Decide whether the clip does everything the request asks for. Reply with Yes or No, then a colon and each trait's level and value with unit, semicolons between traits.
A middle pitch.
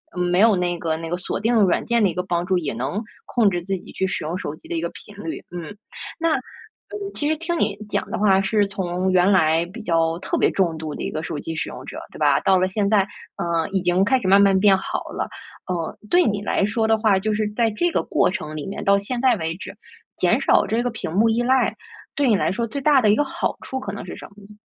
No: high, 195 Hz